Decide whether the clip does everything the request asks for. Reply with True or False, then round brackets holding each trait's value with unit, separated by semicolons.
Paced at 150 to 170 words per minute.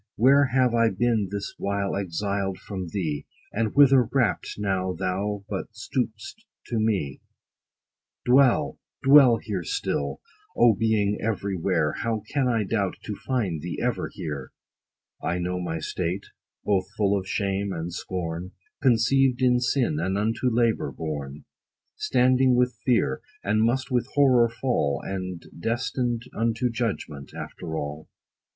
False (140 wpm)